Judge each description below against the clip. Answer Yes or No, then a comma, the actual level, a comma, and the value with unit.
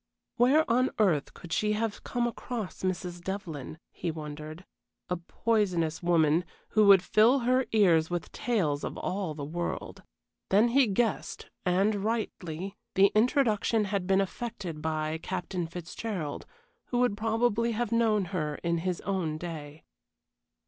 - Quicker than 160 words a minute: No, average, 140 wpm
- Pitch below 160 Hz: No, high, 190 Hz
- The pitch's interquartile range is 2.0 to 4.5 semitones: No, average, 5.1 semitones